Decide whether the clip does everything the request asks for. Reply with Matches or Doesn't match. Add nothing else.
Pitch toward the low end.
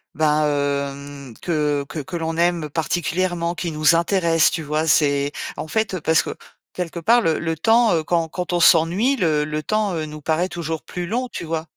Doesn't match